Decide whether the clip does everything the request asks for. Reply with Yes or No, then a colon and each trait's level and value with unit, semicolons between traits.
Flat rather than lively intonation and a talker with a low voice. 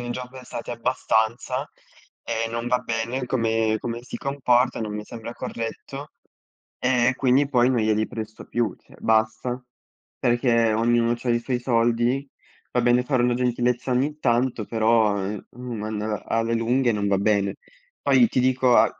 Yes: narrow, 2.0 semitones; low, 120 Hz